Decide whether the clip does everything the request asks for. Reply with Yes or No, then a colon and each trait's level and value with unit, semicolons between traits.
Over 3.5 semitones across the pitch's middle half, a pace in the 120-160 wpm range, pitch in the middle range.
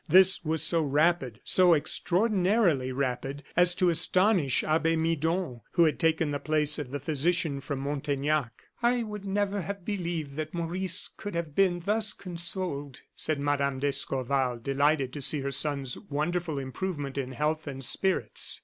Yes: average, 4.2 semitones; average, 155 wpm; medium, 155 Hz